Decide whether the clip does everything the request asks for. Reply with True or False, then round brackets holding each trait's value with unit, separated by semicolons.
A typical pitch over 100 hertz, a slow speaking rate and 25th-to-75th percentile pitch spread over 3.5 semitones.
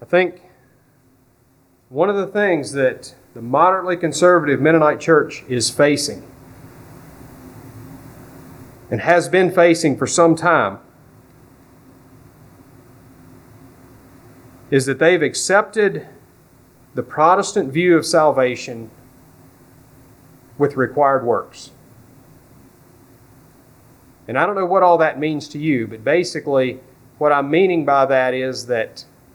True (140 Hz; 105 wpm; 4.6 semitones)